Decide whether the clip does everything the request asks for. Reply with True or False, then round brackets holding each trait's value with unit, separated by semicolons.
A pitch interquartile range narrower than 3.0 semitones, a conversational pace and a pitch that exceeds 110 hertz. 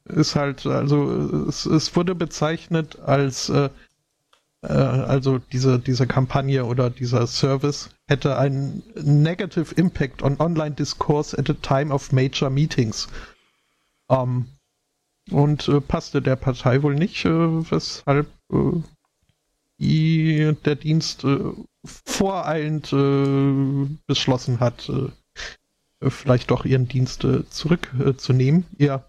False (2.6 semitones; 120 wpm; 140 Hz)